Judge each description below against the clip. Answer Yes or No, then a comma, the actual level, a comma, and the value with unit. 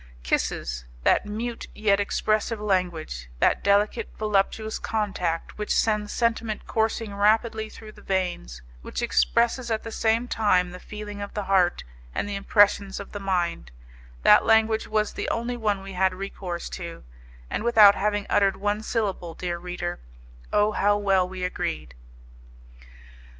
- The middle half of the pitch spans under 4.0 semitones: Yes, average, 2.9 semitones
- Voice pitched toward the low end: No, high, 205 Hz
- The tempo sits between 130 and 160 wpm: Yes, average, 150 wpm